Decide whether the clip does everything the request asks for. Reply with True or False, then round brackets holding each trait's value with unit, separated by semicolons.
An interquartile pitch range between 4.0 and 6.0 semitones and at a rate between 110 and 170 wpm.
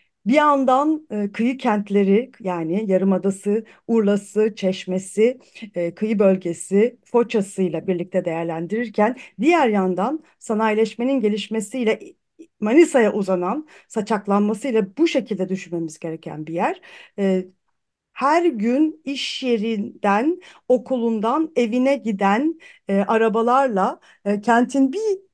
False (5.0 semitones; 100 wpm)